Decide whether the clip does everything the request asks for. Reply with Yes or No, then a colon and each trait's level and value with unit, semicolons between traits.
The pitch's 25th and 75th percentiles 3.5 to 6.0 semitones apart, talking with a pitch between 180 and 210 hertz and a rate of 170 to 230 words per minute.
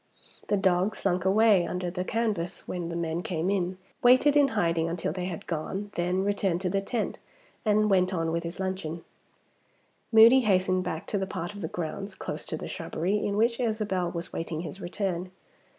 No: average, 3.0 semitones; medium, 185 Hz; average, 190 wpm